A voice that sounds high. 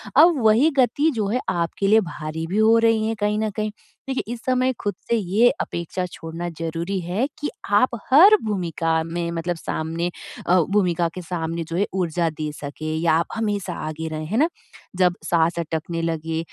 No: medium, 175 Hz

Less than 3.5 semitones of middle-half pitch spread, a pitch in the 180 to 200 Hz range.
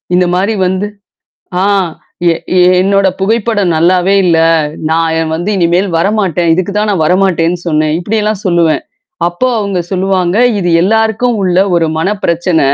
Yes: average, 2.8 semitones; medium, 185 Hz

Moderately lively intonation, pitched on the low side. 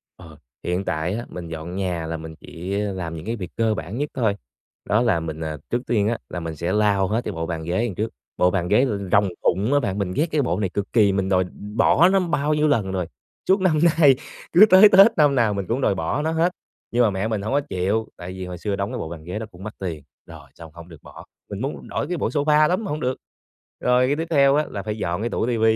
No: wide, 6.9 semitones; low, 105 Hz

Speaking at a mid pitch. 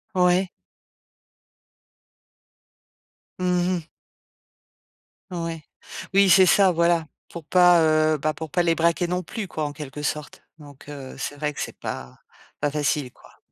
Yes: medium, 165 Hz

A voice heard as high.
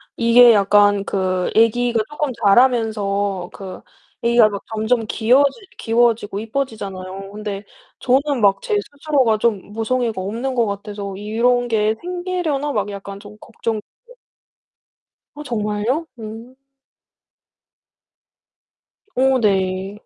Yes: high, 220 Hz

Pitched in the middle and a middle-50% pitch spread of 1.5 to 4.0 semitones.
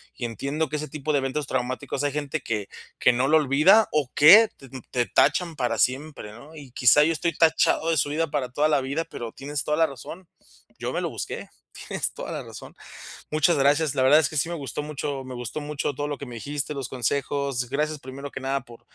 Yes: medium, 145 Hz; average, 2.8 semitones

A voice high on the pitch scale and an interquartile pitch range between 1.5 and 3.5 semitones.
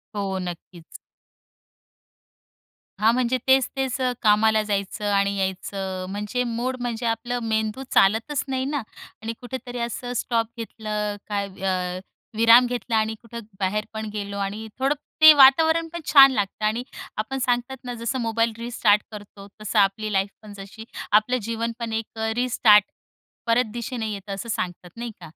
Yes: high, 220 Hz; average, 3.1 semitones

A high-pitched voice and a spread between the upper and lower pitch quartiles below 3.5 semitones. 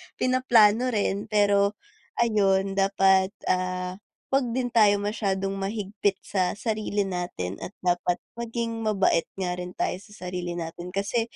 Yes: high, 200 Hz; average, 2.8 semitones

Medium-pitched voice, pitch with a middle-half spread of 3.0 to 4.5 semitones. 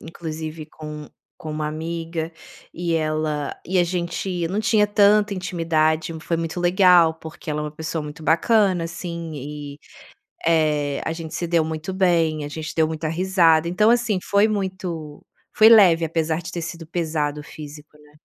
No: medium, 165 Hz; narrow, 2.4 semitones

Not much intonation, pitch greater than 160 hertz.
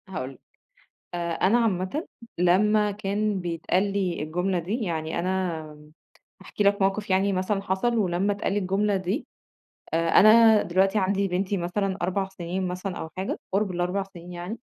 Yes: narrow, 2.3 semitones; high, 190 Hz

